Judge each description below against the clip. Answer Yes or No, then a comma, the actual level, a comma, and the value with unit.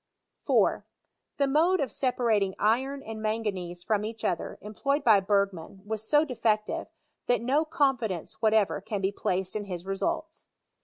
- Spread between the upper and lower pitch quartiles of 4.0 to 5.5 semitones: Yes, average, 5.2 semitones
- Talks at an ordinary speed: Yes, average, 155 wpm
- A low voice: No, high, 220 Hz